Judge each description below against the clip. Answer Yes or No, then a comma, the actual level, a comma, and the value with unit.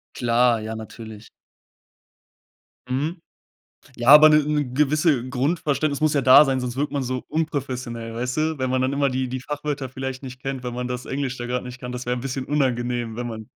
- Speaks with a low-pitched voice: Yes, low, 130 Hz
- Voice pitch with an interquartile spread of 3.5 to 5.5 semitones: No, narrow, 2.6 semitones